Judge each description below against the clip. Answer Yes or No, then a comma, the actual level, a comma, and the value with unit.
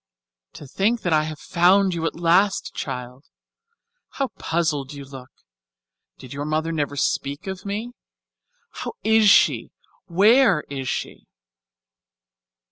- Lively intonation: Yes, wide, 5.7 semitones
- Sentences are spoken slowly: Yes, slow, 125 wpm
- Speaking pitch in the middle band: Yes, medium, 165 Hz